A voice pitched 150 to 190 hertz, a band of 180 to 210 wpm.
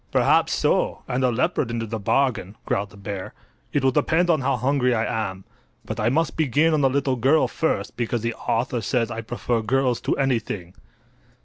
No: low, 125 Hz; average, 195 wpm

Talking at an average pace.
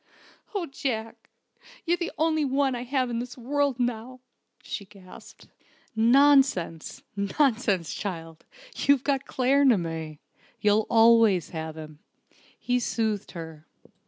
No: slow, 115 wpm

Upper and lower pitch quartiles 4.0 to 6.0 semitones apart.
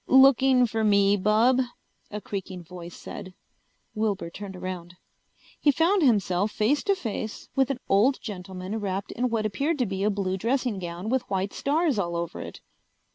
Yes: average, 5.1 semitones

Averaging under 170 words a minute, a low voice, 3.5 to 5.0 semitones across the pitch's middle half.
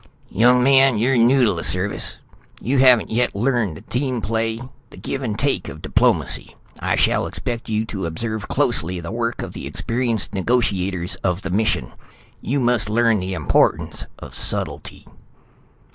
Yes: average, 160 wpm; low, 115 Hz; average, 4.3 semitones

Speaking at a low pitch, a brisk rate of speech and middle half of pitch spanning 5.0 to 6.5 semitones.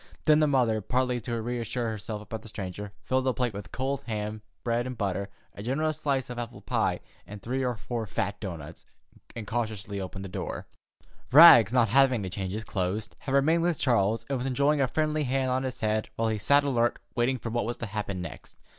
No: low, 120 Hz; fast, 215 wpm; average, 3.8 semitones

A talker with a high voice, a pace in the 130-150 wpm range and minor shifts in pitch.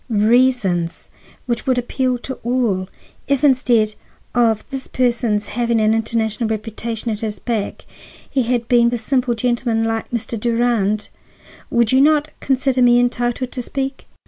Yes: high, 235 Hz; average, 145 wpm; narrow, 2.3 semitones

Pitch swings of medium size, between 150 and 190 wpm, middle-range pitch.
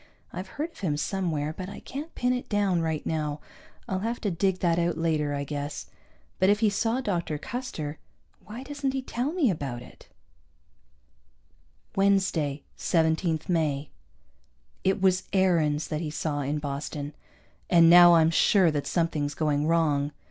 Yes: average, 4.7 semitones; average, 160 wpm; medium, 165 Hz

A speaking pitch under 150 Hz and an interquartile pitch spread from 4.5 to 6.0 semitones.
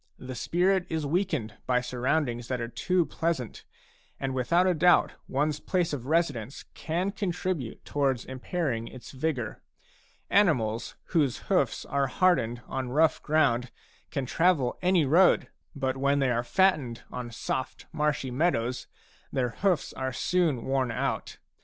Yes: medium, 140 Hz; average, 5.3 semitones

